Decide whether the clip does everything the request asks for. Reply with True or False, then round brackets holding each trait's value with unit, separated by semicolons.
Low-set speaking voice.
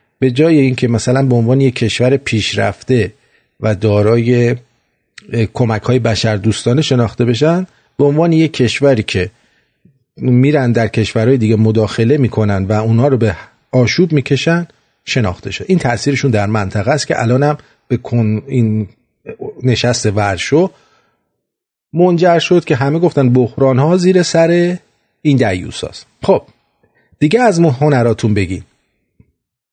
True (125 Hz)